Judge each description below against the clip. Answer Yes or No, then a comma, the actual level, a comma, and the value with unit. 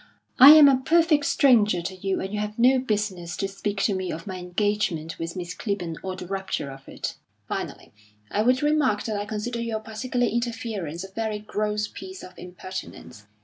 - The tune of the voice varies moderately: Yes, average, 4.1 semitones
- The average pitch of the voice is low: No, high, 210 Hz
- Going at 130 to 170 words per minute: No, average, 190 wpm